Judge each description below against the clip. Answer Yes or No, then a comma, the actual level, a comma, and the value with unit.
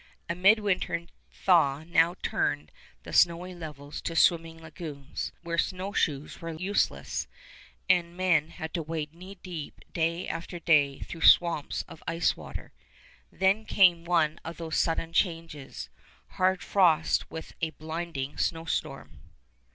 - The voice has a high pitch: No, medium, 165 Hz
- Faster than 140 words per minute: No, slow, 135 wpm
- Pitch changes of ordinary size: No, narrow, 2.1 semitones